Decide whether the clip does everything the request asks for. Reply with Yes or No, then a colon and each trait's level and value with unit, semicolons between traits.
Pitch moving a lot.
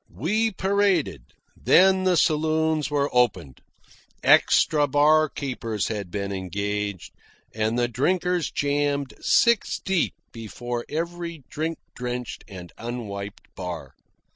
Yes: wide, 7.4 semitones